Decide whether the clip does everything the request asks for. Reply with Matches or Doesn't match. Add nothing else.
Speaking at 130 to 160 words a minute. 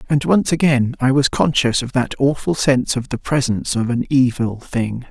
Doesn't match